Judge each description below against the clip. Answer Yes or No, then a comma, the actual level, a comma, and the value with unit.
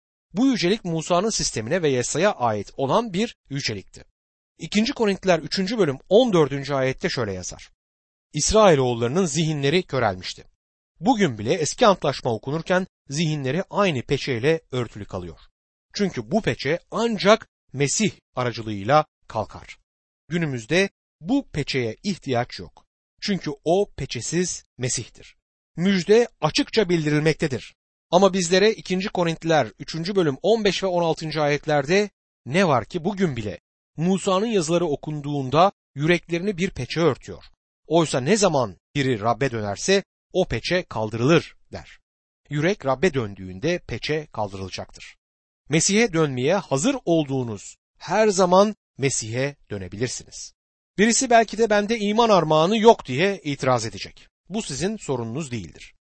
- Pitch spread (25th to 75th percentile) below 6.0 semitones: No, wide, 7.5 semitones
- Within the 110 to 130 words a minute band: Yes, average, 120 wpm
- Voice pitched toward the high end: No, medium, 155 Hz